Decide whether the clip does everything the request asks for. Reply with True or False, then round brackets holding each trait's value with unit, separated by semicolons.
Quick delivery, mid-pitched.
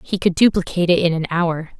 True (235 wpm; 175 Hz)